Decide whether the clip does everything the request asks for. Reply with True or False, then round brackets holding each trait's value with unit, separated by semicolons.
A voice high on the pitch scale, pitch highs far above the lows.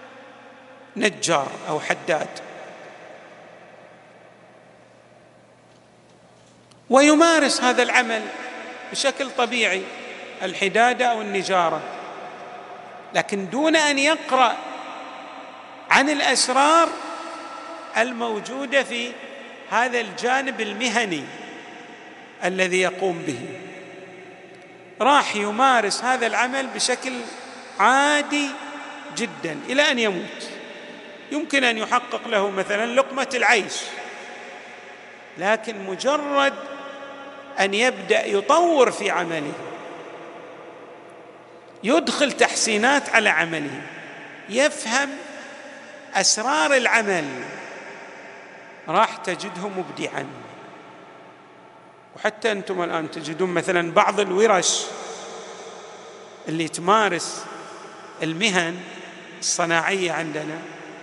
True (220 Hz; 6.7 semitones)